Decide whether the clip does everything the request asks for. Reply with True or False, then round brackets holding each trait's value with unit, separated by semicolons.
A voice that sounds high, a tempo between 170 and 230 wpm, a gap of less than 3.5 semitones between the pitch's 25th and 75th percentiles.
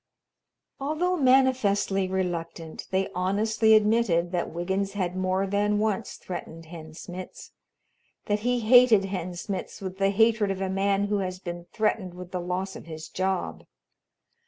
False (195 Hz; 150 wpm; 2.9 semitones)